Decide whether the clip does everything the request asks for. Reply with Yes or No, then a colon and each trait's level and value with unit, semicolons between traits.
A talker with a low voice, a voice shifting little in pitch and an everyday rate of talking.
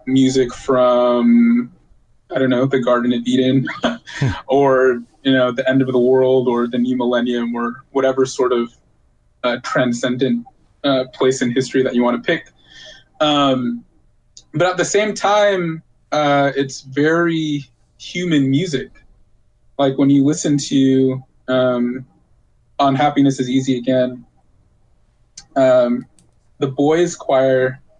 No: low, 130 Hz; narrow, 2.1 semitones; slow, 130 wpm